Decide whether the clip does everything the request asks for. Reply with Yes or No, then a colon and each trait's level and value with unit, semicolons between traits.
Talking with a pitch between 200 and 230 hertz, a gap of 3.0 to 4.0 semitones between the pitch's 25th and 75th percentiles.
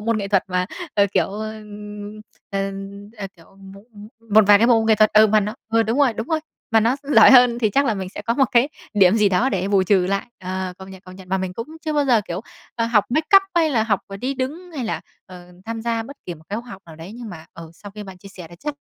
Yes: high, 210 Hz; average, 3.7 semitones